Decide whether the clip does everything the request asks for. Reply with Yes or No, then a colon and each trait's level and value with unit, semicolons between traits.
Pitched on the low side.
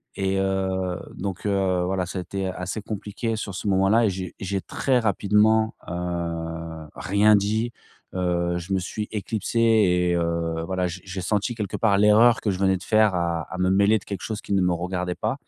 Yes: very low, 95 Hz